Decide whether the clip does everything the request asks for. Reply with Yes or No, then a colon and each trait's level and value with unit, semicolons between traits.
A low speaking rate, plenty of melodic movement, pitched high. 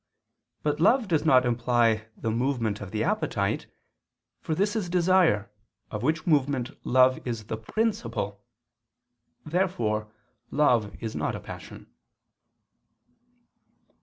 No: slow, 115 wpm; wide, 6.6 semitones; low, 130 Hz